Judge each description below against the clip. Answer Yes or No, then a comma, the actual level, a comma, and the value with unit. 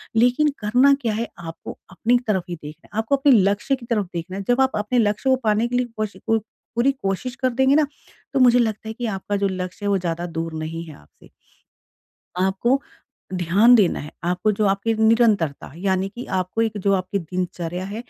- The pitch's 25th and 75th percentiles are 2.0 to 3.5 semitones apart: No, average, 4.6 semitones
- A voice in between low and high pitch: No, high, 210 Hz